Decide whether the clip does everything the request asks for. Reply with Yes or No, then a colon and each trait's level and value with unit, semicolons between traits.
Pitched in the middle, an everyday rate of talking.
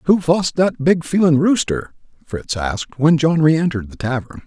Yes: medium, 150 Hz; average, 175 wpm